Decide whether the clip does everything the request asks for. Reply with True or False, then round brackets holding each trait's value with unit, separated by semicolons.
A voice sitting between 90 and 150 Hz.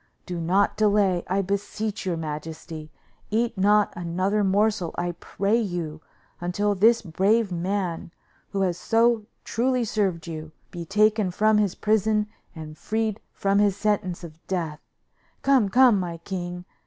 False (195 Hz)